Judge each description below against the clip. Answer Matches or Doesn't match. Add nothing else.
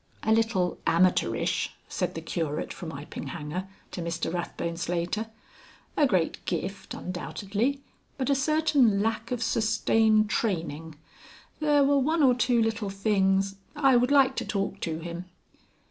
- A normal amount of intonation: Doesn't match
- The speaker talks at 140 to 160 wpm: Matches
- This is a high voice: Matches